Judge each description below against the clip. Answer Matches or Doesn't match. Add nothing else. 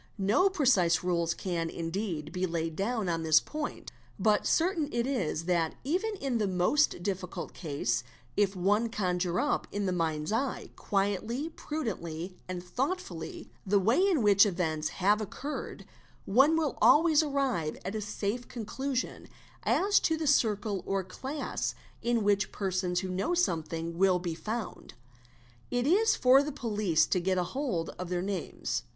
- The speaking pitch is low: Doesn't match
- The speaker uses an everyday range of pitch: Doesn't match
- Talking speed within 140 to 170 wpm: Matches